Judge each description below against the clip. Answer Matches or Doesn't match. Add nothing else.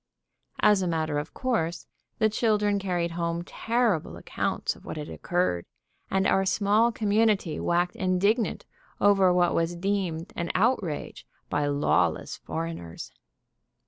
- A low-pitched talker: Doesn't match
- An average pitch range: Matches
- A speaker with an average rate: Doesn't match